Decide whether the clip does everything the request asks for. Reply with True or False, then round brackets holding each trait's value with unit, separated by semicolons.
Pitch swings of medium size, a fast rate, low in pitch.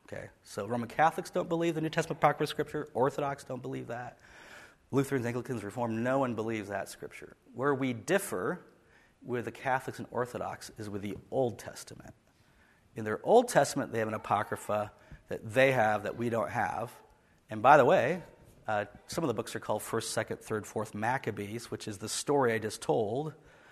False (4.2 semitones; 185 wpm; 115 Hz)